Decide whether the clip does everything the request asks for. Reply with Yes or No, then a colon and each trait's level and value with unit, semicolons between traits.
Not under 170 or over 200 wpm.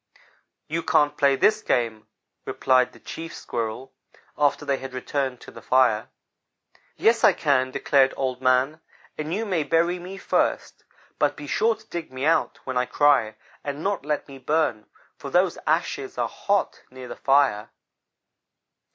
No: average, 160 wpm